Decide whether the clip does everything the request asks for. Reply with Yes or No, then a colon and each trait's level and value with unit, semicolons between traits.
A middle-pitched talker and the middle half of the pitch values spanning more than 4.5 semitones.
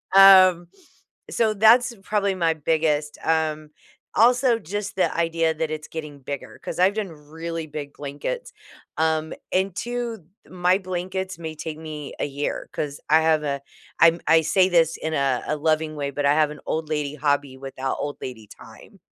No: medium, 160 Hz; average, 3.9 semitones